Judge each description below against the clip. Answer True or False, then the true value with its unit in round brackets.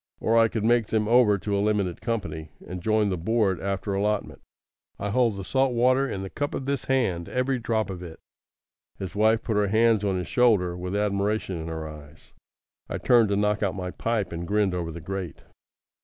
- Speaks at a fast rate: True (210 wpm)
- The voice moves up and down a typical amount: True (3.8 semitones)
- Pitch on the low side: True (105 Hz)